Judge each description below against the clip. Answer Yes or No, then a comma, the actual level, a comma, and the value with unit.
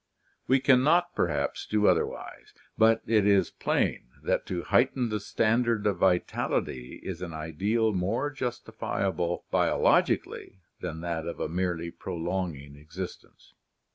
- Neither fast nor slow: No, slow, 130 wpm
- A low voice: Yes, very low, 95 Hz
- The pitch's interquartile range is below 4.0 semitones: No, average, 5.0 semitones